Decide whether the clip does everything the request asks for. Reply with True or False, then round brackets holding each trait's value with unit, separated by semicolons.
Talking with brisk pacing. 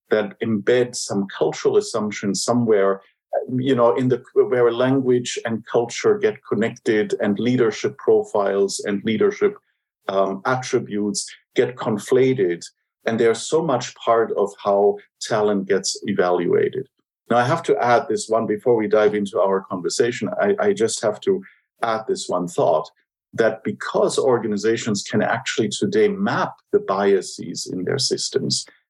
False (145 wpm)